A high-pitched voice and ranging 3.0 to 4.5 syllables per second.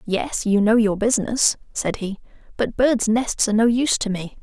No: high, 220 Hz; 5.0 syllables/s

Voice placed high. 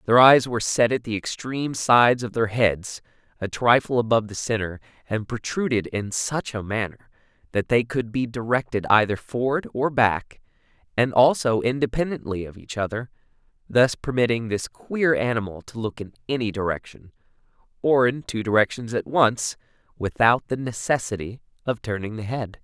No: low, 115 Hz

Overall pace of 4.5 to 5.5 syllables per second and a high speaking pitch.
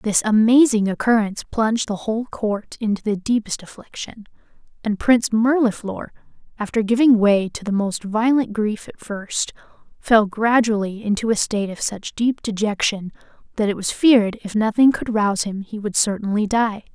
Yes: 5.0 syllables/s; high, 215 Hz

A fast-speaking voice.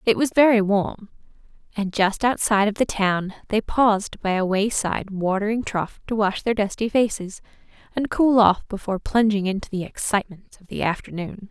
No: average, 170 wpm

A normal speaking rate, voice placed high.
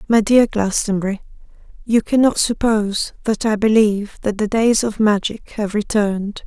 Yes: average, 150 wpm; high, 215 Hz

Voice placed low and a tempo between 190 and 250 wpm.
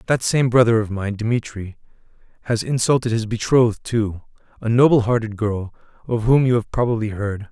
No: low, 115 Hz; average, 170 wpm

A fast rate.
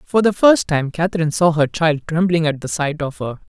Yes: fast, 235 wpm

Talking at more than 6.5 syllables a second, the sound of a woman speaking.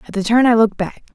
Yes: 7.7 syllables/s; female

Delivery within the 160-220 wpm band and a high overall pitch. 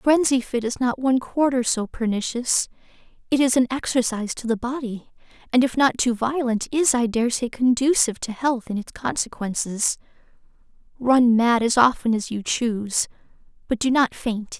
Yes: average, 170 wpm; high, 245 Hz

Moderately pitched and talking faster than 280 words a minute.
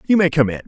Yes: medium, 155 Hz; fast, 360 wpm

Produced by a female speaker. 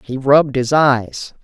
Yes: female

